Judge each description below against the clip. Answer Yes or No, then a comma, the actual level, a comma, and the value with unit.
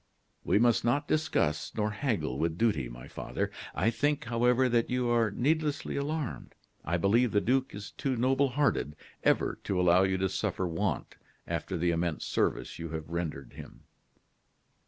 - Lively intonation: Yes, wide, 6.9 semitones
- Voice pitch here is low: Yes, low, 110 Hz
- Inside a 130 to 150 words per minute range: No, average, 165 wpm